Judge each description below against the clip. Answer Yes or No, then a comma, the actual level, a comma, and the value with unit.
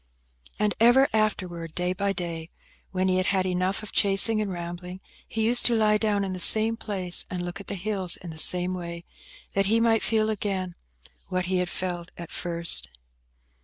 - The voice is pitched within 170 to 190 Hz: Yes, medium, 185 Hz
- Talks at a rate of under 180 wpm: No, average, 195 wpm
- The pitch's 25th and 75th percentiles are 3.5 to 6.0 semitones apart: No, average, 3.1 semitones